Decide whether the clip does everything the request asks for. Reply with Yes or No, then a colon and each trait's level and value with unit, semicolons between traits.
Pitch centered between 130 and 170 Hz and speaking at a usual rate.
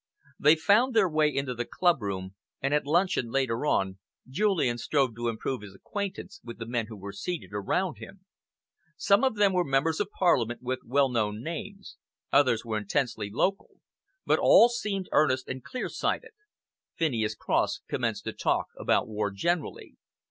Yes: low, 135 Hz; average, 170 wpm